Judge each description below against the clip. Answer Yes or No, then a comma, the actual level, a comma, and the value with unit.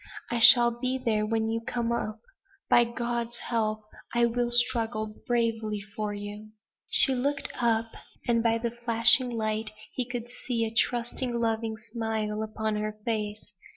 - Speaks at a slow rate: No, average, 155 wpm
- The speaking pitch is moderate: No, high, 230 Hz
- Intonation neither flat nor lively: No, narrow, 1.7 semitones